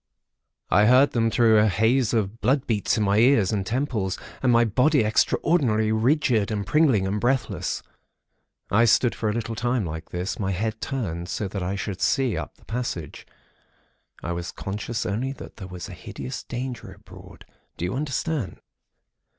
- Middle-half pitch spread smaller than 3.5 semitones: No, average, 4.2 semitones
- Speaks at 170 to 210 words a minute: Yes, average, 175 wpm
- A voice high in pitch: No, low, 110 Hz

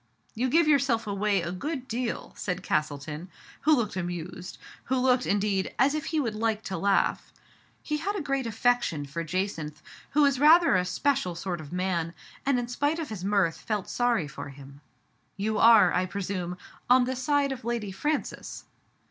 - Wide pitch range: Yes, wide, 6.4 semitones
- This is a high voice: Yes, high, 210 Hz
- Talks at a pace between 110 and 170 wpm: No, average, 190 wpm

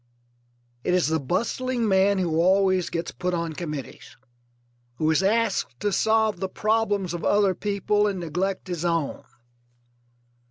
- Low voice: No, medium, 185 Hz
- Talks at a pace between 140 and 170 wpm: Yes, average, 145 wpm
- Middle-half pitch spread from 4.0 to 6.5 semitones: No, average, 3.5 semitones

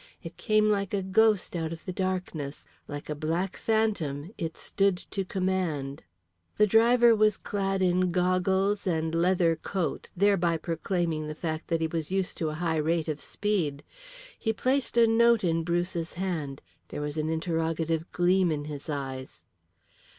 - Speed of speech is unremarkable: Yes, average, 165 wpm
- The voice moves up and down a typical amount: Yes, average, 3.5 semitones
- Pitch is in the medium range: Yes, medium, 175 Hz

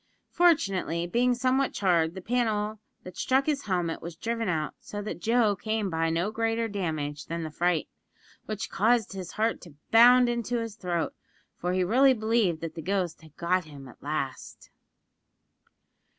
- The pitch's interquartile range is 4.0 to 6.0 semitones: Yes, average, 5.3 semitones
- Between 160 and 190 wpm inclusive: Yes, average, 165 wpm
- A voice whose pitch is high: Yes, high, 195 Hz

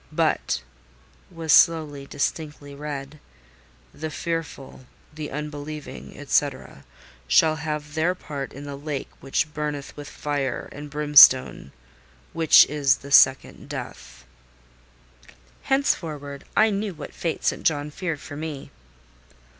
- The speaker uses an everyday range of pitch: No, narrow, 1.9 semitones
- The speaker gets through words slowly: Yes, slow, 115 wpm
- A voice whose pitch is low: No, medium, 150 Hz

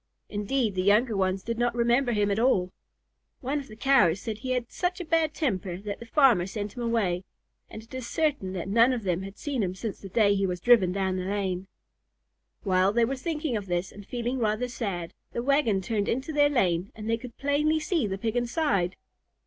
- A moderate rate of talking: No, fast, 220 wpm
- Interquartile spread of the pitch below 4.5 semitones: No, average, 5.0 semitones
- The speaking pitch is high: Yes, high, 225 Hz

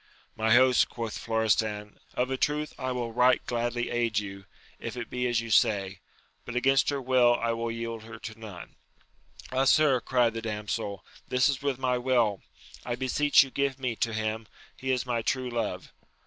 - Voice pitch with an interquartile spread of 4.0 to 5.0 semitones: No, narrow, 2.4 semitones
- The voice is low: Yes, low, 120 Hz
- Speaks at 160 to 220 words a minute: Yes, average, 190 wpm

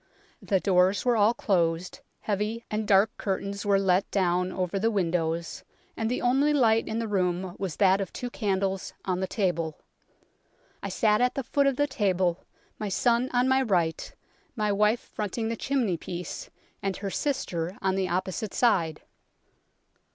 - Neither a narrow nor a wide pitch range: Yes, average, 3.8 semitones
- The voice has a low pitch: No, high, 200 Hz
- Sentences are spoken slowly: No, average, 165 wpm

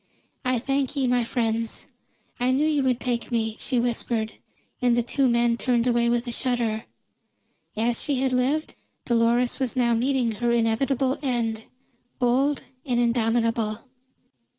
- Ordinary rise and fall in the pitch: No, narrow, 1.8 semitones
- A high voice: Yes, high, 240 Hz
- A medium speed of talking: Yes, average, 150 wpm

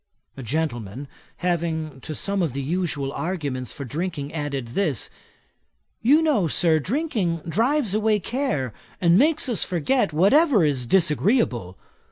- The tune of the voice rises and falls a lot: Yes, wide, 6.9 semitones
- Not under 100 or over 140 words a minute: Yes, slow, 135 wpm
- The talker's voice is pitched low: No, medium, 165 Hz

